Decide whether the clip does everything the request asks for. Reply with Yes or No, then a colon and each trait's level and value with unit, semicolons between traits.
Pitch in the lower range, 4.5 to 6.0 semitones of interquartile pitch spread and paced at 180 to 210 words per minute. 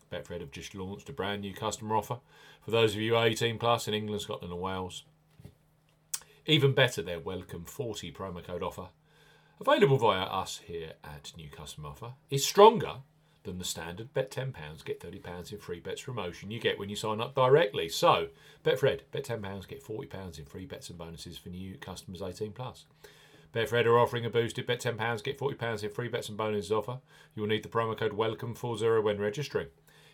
Yes: low, 115 Hz; average, 4.9 semitones; average, 190 wpm